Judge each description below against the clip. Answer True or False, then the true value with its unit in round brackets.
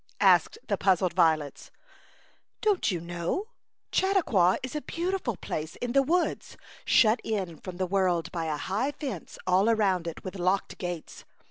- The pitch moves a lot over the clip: True (6.9 semitones)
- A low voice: False (190 Hz)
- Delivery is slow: False (160 wpm)